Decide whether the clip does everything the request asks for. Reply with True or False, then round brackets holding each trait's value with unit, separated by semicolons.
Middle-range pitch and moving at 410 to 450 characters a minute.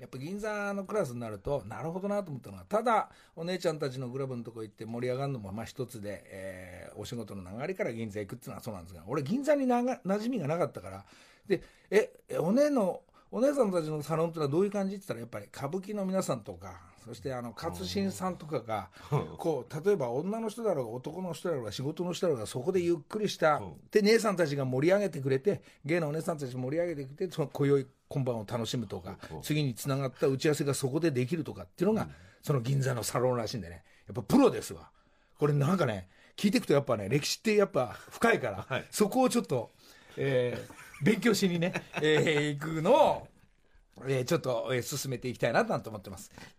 True (145 Hz; 440 characters per minute)